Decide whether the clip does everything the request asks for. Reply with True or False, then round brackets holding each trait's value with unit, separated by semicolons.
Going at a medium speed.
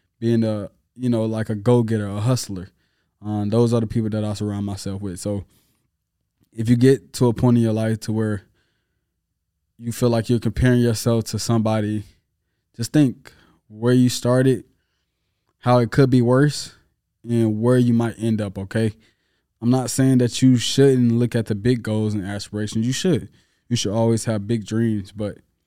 True (185 wpm)